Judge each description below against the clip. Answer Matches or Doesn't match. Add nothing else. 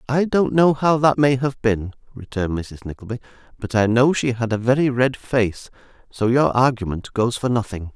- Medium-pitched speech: Doesn't match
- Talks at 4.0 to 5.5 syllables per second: Matches